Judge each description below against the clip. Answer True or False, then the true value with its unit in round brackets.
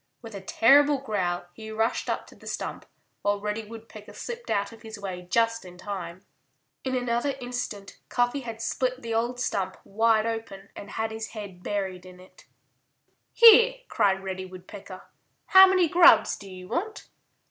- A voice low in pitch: False (220 Hz)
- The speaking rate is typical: True (170 wpm)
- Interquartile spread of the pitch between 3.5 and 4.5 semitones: True (4.1 semitones)